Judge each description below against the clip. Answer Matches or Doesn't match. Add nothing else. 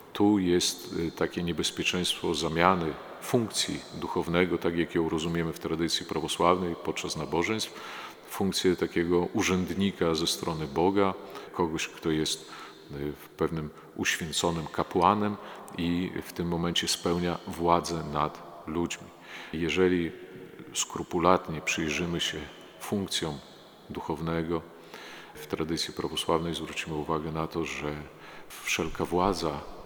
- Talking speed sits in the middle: Doesn't match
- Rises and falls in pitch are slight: Matches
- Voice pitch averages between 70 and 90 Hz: Matches